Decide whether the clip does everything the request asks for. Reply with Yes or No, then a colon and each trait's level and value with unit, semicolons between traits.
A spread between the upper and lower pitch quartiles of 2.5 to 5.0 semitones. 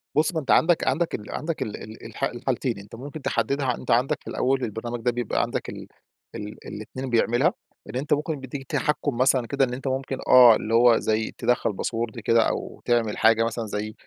Yes: average, 3.0 semitones